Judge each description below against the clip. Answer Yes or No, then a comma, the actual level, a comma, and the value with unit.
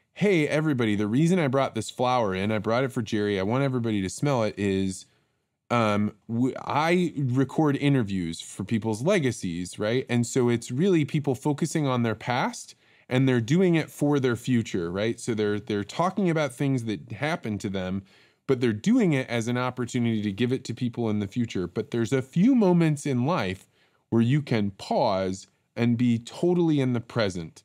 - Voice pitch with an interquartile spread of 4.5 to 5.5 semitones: Yes, average, 4.9 semitones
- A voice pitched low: Yes, low, 120 Hz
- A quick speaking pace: No, average, 190 wpm